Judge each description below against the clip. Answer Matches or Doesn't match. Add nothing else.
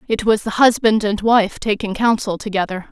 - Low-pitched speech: Doesn't match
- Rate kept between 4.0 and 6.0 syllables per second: Matches